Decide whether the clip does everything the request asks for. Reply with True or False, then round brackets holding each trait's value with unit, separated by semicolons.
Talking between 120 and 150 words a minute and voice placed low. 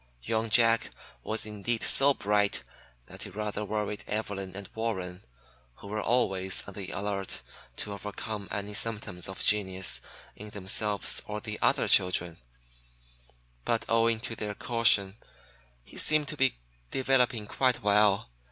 True (135 wpm; 105 Hz)